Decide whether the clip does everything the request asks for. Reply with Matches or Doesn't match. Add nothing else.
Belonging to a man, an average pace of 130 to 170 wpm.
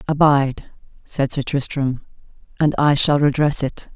Doesn't match